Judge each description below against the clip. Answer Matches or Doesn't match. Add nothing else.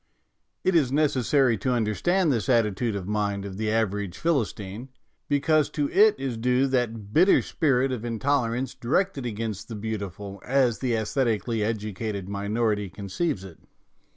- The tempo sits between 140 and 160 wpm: Matches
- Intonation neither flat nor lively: Matches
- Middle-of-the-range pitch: Doesn't match